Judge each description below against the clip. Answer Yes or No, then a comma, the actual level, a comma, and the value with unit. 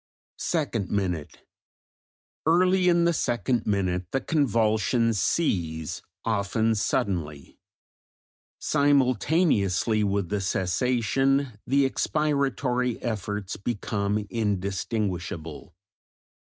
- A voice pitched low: Yes, low, 110 Hz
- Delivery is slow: Yes, slow, 75 wpm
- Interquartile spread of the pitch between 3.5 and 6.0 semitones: Yes, wide, 5.4 semitones